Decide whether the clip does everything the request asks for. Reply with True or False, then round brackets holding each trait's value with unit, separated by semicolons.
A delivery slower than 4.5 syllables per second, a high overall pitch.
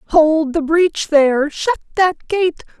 True (3.6 syllables/s; 320 Hz)